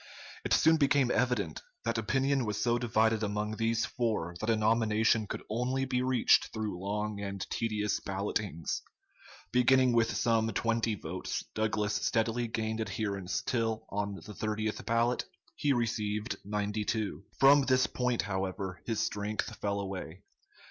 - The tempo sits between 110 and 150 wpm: Yes, average, 140 wpm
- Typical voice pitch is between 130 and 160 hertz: No, low, 110 Hz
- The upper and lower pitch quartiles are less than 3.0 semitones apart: Yes, narrow, 2.4 semitones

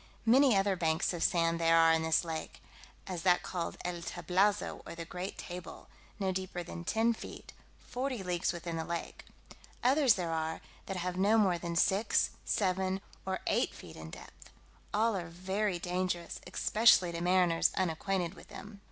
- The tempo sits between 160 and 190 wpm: Yes, average, 170 wpm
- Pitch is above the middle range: No, medium, 180 Hz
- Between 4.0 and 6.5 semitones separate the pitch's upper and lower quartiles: No, narrow, 2.6 semitones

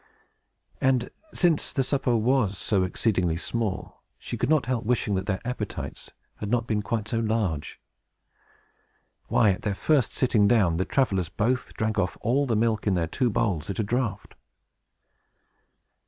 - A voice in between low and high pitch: No, low, 110 Hz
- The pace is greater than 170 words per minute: No, average, 165 wpm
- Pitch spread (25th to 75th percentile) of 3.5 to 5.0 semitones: Yes, average, 3.9 semitones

